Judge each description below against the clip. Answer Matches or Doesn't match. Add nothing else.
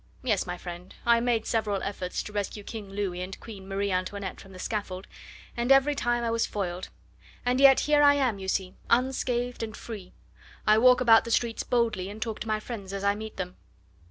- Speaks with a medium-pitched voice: Doesn't match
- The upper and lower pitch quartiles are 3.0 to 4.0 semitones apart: Matches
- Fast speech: Matches